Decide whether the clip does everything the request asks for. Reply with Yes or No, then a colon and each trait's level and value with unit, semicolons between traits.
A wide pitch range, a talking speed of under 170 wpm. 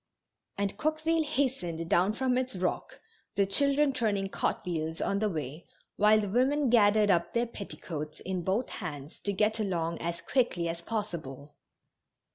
Yes: wide, 6.1 semitones; average, 150 wpm